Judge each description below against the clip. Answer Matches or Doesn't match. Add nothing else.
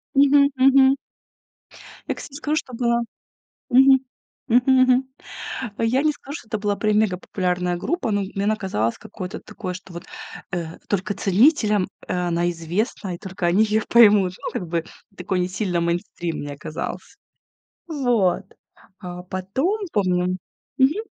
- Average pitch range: Doesn't match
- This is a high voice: Matches